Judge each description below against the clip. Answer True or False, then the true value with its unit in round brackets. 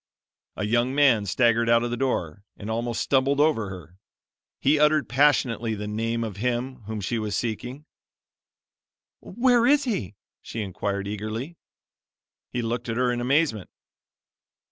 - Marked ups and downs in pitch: False (4.0 semitones)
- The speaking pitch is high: False (120 Hz)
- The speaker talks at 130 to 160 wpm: True (145 wpm)